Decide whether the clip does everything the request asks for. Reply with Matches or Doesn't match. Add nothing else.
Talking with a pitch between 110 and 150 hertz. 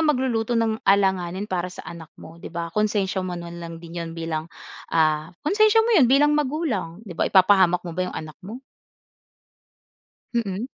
Doesn't match